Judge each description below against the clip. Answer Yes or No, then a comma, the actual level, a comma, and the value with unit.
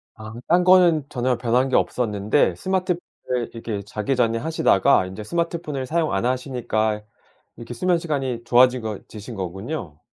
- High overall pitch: No, low, 125 Hz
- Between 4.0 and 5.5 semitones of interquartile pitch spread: No, wide, 6.2 semitones